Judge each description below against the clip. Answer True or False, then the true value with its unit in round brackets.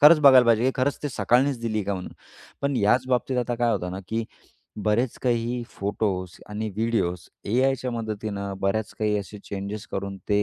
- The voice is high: False (110 Hz)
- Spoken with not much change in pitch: False (3.5 semitones)